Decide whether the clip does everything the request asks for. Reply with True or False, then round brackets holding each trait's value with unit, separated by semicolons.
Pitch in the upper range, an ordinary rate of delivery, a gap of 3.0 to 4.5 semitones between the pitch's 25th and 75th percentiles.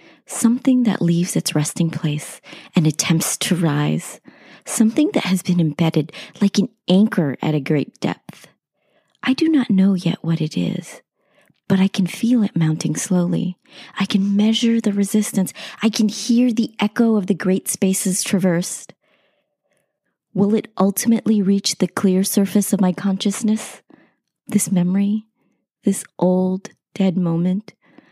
True (195 Hz; 145 wpm; 3.5 semitones)